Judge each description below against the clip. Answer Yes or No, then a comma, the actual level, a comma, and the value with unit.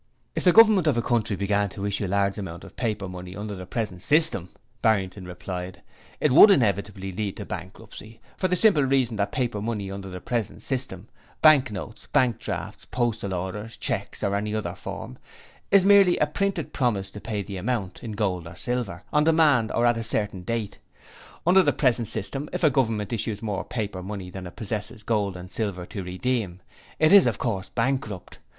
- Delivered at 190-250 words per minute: Yes, average, 195 wpm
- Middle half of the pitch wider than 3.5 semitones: Yes, average, 4.7 semitones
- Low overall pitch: Yes, low, 105 Hz